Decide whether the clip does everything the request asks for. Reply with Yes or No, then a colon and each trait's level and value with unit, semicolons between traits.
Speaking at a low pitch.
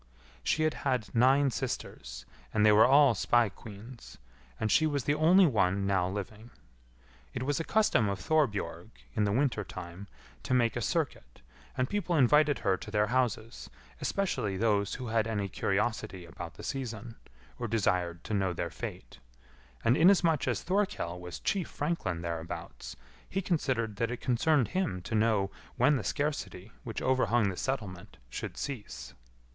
Yes: low, 115 Hz